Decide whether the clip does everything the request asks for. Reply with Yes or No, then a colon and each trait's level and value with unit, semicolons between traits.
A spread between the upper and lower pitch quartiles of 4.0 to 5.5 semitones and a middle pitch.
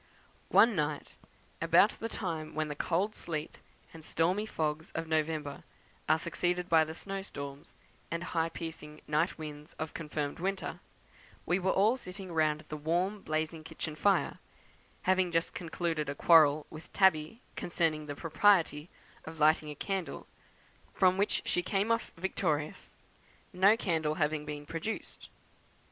No: average, 3.2 semitones; medium, 160 Hz